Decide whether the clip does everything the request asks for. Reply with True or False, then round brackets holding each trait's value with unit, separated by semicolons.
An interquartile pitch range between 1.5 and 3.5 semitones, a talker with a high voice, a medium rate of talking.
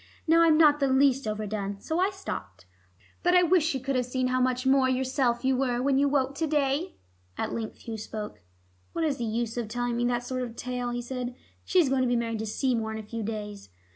False (3.2 semitones; 255 Hz; 240 wpm)